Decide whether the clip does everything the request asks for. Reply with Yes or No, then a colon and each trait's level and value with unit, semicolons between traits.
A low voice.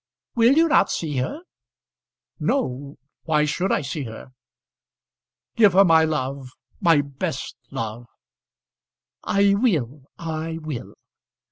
No: medium, 155 Hz